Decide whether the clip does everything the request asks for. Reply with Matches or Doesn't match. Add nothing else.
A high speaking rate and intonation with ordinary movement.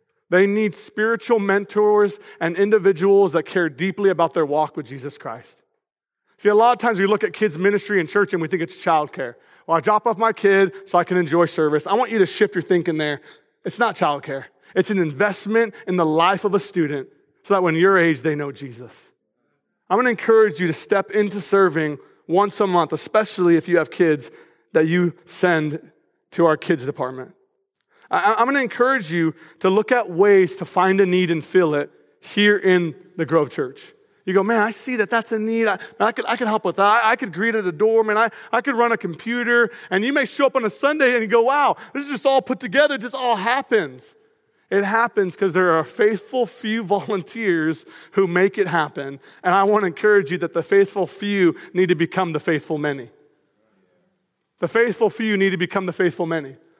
Matches